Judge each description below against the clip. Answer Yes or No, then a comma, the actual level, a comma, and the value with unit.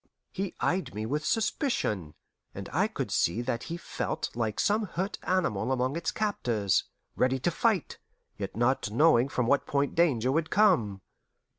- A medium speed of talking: Yes, average, 160 wpm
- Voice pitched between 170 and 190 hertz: No, low, 135 Hz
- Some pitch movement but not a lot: No, wide, 7.8 semitones